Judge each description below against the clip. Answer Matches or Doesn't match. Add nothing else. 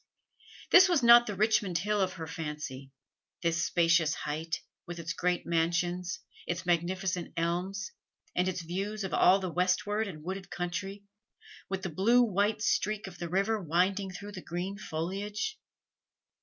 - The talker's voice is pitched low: Doesn't match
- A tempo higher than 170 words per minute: Doesn't match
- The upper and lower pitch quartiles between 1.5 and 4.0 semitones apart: Matches